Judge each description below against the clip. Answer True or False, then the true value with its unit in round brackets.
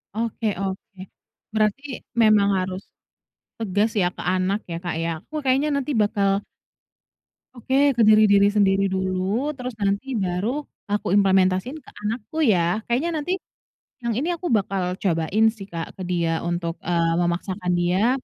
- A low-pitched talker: False (200 Hz)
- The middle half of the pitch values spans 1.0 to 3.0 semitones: False (3.7 semitones)